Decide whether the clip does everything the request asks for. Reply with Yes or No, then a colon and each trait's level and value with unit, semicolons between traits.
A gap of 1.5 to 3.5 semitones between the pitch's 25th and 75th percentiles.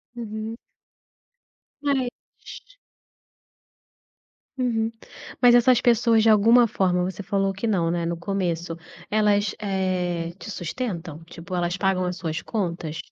No: average, 4.4 semitones